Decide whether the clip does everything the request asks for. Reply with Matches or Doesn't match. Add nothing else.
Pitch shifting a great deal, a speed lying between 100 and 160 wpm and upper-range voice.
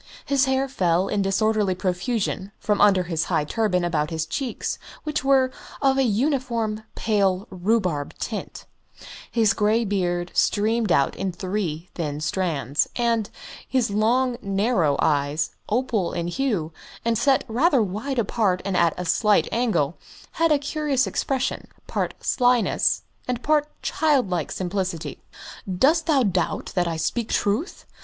Matches